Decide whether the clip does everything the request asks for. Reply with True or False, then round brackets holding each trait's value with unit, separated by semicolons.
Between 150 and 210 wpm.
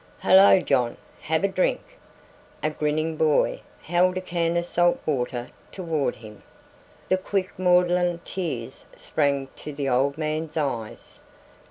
False (135 wpm)